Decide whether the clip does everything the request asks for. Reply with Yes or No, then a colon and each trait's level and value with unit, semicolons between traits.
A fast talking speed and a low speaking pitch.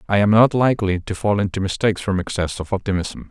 Yes: fast, 220 wpm; low, 100 Hz